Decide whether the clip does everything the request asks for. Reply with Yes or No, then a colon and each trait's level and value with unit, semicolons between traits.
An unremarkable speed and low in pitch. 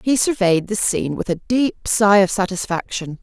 No: average, 185 wpm; high, 200 Hz